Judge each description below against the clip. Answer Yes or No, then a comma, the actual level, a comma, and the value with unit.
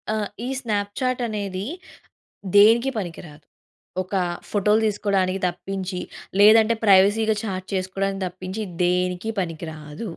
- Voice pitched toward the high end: Yes, high, 195 Hz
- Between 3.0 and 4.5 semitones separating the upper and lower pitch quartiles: No, narrow, 2.6 semitones